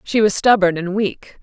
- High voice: Yes, high, 200 Hz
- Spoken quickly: Yes, fast, 210 wpm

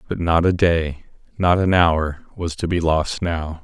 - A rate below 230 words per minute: Yes, average, 200 wpm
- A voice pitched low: Yes, very low, 85 Hz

